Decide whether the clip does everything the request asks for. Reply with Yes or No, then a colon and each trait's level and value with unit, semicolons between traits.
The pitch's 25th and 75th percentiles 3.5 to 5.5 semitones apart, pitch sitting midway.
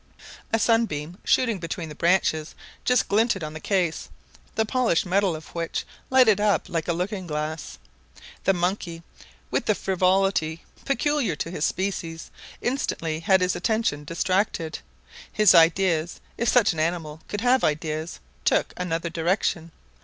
Yes: average, 4.1 semitones; medium, 180 Hz